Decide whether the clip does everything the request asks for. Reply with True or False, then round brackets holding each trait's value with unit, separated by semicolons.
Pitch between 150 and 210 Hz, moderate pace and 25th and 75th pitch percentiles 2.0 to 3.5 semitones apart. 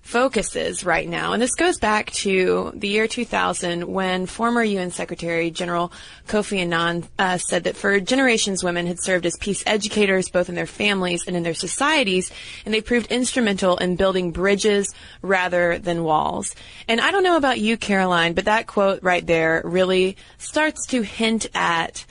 False (190 Hz; 175 wpm; 4.0 semitones)